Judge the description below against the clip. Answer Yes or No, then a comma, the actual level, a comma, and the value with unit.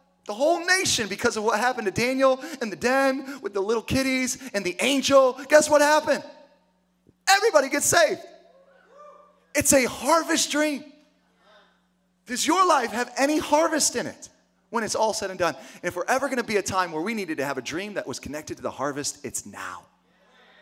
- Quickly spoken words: No, average, 195 wpm